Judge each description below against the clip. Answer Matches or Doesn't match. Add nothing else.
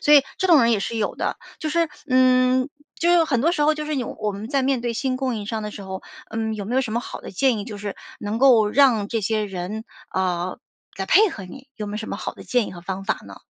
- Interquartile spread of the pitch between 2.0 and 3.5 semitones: Doesn't match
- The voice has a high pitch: Matches